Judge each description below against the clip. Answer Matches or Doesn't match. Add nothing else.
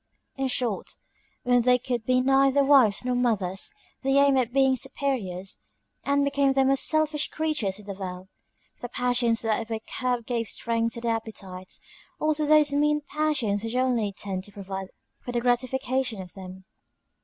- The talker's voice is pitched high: Matches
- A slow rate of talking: Doesn't match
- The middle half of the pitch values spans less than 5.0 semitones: Matches